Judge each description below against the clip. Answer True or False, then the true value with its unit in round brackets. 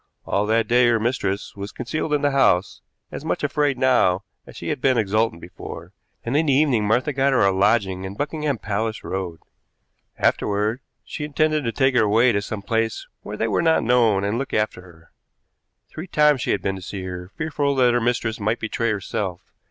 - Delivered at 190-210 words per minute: True (205 wpm)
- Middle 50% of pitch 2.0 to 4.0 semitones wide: False (5.2 semitones)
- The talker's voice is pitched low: True (115 Hz)